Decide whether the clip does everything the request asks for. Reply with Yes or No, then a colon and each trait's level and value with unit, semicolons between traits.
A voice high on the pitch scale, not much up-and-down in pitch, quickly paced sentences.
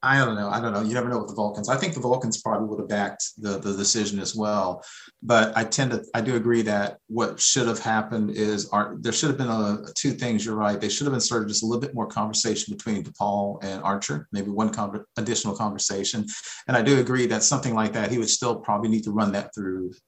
No: low, 110 Hz; narrow, 2.3 semitones; fast, 255 wpm